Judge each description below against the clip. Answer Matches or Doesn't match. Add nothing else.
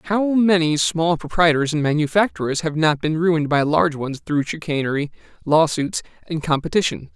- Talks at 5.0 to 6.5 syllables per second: Matches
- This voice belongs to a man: Matches